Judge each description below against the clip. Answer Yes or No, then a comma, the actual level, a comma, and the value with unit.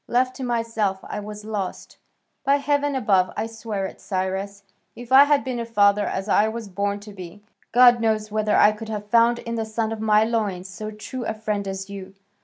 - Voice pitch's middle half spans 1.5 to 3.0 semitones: Yes, narrow, 2.4 semitones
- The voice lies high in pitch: Yes, high, 215 Hz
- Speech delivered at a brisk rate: Yes, fast, 210 wpm